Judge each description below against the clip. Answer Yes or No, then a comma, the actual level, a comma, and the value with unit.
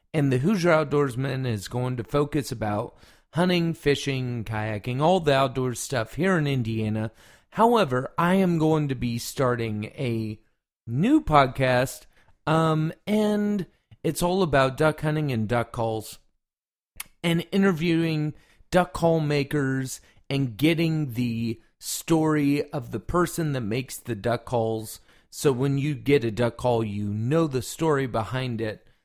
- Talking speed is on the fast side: No, average, 145 wpm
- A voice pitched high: No, low, 135 Hz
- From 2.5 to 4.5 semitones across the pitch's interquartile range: No, wide, 5.4 semitones